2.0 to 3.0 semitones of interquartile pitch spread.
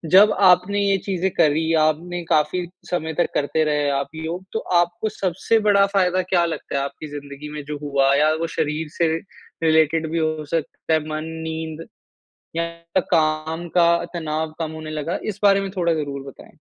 Yes: narrow, 2.4 semitones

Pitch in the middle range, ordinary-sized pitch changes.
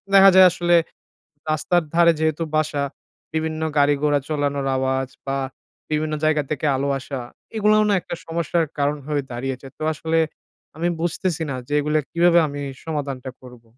Yes: medium, 150 Hz; average, 3.0 semitones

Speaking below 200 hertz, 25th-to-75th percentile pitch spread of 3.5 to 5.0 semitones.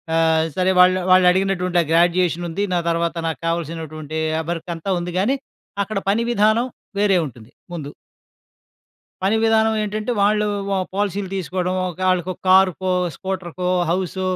No: medium, 185 Hz; average, 2.8 semitones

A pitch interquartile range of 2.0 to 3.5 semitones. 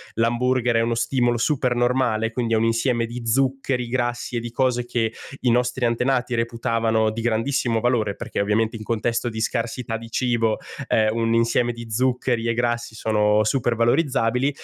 No: narrow, 1.5 semitones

